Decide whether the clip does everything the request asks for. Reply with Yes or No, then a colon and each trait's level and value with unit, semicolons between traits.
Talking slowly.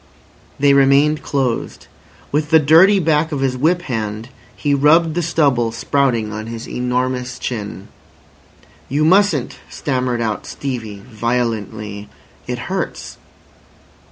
Yes: slow, 120 wpm